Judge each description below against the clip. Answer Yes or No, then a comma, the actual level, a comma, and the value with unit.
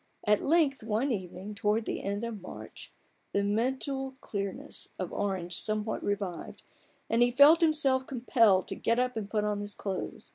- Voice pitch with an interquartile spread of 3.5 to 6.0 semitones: Yes, average, 4.3 semitones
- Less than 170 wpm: No, average, 175 wpm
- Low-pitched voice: No, high, 215 Hz